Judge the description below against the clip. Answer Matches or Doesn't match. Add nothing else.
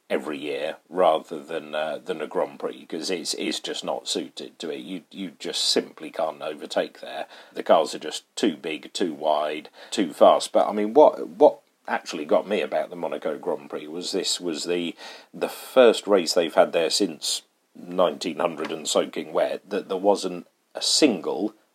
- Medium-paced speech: Matches